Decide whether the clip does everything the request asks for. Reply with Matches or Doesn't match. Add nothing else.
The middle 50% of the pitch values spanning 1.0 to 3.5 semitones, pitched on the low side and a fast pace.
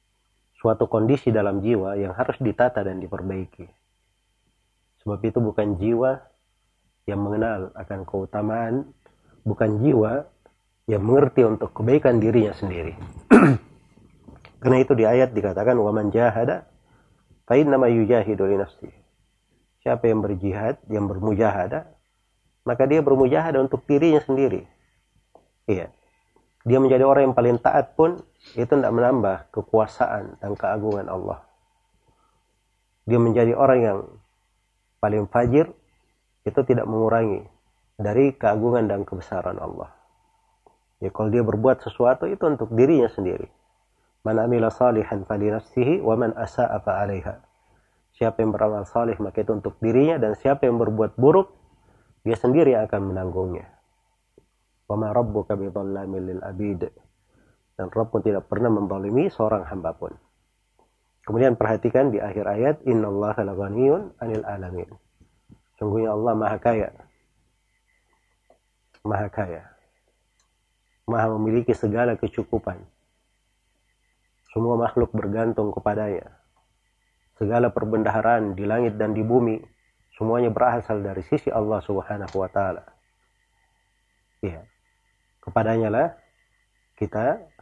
Doesn't match